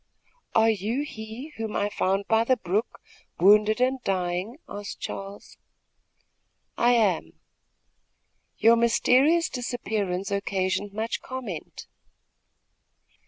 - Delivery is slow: Yes, slow, 100 wpm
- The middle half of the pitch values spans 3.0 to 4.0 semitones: Yes, average, 3.5 semitones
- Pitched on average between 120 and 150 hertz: No, high, 220 Hz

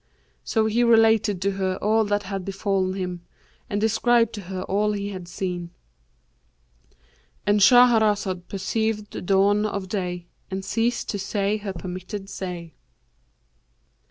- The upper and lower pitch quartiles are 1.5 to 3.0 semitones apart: Yes, narrow, 2.6 semitones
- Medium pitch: No, high, 195 Hz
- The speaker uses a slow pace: Yes, slow, 130 wpm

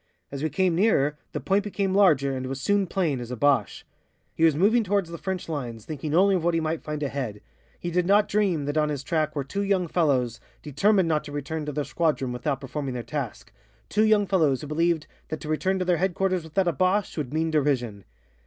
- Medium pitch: Yes, medium, 155 Hz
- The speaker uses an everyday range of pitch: Yes, average, 4.9 semitones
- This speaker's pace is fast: Yes, fast, 225 wpm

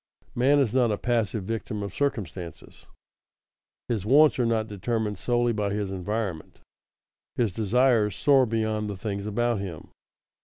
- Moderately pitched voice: No, low, 110 Hz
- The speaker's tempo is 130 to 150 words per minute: Yes, average, 145 wpm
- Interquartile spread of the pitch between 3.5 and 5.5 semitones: No, average, 3.1 semitones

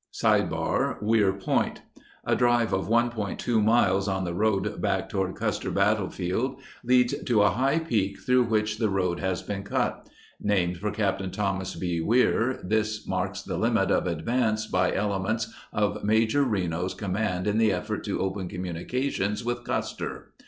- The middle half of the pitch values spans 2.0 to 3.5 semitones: Yes, average, 3.1 semitones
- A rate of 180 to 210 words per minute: No, average, 165 wpm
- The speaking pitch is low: Yes, low, 105 Hz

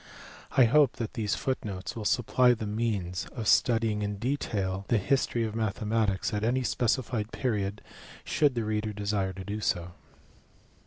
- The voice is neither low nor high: No, low, 110 Hz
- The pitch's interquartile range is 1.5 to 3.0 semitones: Yes, average, 2.7 semitones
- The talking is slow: No, average, 155 wpm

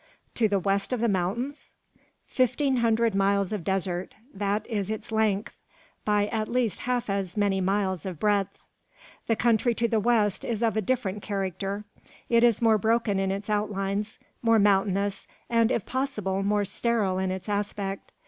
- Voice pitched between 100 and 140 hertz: No, high, 205 Hz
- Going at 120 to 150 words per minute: No, average, 165 wpm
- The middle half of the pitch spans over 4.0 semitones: No, average, 2.7 semitones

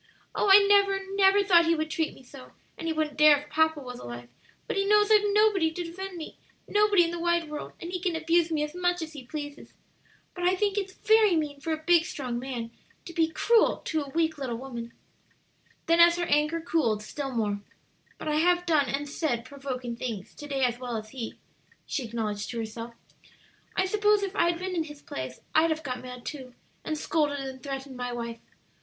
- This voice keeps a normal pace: No, fast, 215 wpm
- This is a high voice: Yes, very high, 310 Hz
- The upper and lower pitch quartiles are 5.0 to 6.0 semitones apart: Yes, wide, 5.4 semitones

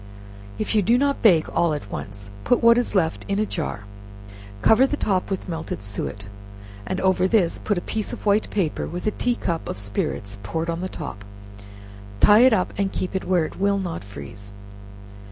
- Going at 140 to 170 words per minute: No, average, 200 wpm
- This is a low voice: No, medium, 180 Hz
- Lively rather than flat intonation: Yes, wide, 6.2 semitones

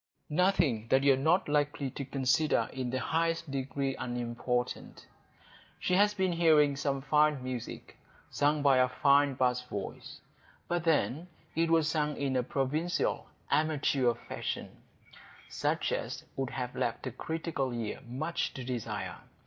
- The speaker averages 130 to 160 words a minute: Yes, average, 140 wpm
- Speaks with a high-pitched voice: No, medium, 140 Hz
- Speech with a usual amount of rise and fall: Yes, average, 3.7 semitones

